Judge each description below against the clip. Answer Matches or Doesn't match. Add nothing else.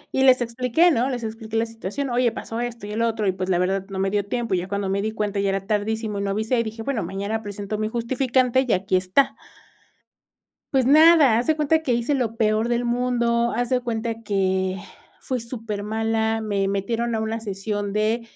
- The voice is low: Doesn't match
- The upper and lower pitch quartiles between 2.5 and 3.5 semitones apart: Matches